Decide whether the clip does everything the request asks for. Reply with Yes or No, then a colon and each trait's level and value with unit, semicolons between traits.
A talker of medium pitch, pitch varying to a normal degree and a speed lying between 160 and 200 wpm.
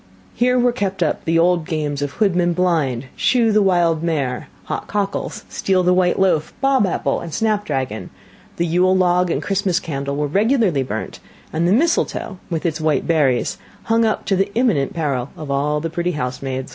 Yes: medium, 170 Hz; average, 4.8 semitones; average, 185 wpm